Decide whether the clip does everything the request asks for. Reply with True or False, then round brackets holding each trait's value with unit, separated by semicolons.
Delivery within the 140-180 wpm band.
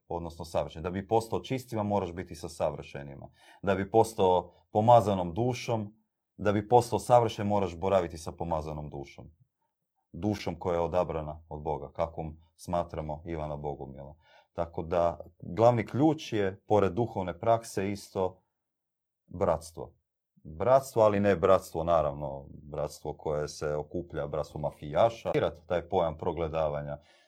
False (130 wpm)